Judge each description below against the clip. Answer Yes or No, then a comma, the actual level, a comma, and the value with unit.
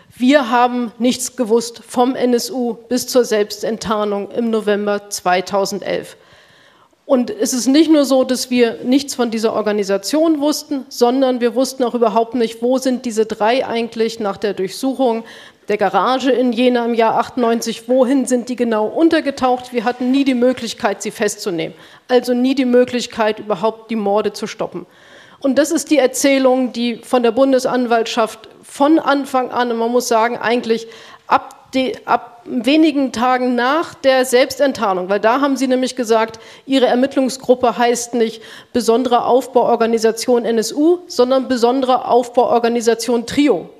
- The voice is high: Yes, high, 245 Hz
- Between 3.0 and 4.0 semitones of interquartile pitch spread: No, narrow, 2.4 semitones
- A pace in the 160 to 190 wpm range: No, average, 150 wpm